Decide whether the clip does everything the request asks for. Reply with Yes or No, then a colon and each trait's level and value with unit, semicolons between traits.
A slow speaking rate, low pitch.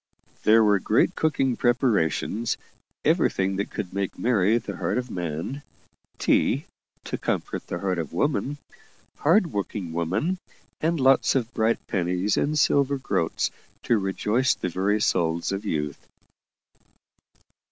Yes: slow, 130 wpm; low, 105 Hz